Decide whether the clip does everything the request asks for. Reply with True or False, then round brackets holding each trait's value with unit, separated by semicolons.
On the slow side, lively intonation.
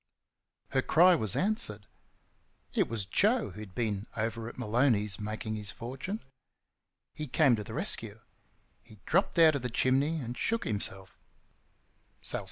False (145 wpm; 6.3 semitones)